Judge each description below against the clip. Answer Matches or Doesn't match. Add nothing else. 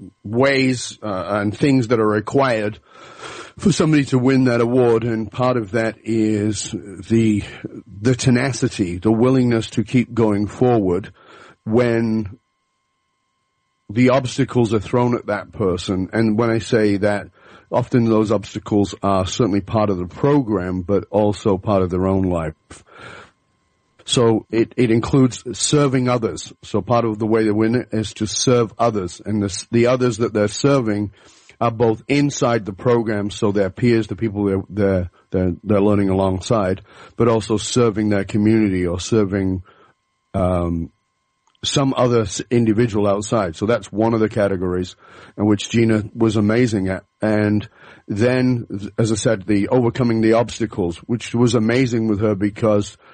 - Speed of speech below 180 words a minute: Matches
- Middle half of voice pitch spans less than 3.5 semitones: Matches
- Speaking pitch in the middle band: Doesn't match